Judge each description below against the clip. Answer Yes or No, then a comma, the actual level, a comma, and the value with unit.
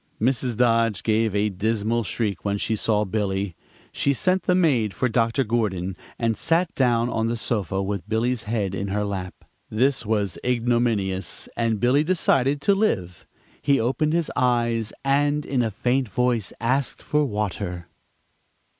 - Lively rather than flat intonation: No, average, 3.6 semitones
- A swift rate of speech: No, average, 155 wpm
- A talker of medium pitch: No, low, 115 Hz